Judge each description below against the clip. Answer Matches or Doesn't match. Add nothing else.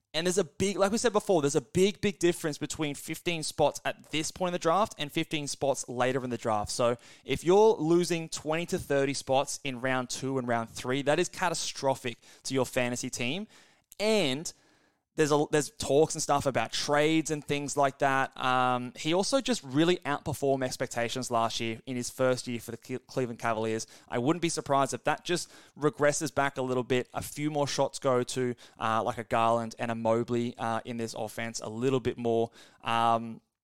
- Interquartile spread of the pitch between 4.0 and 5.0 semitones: Matches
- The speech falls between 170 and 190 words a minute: Doesn't match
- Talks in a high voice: Doesn't match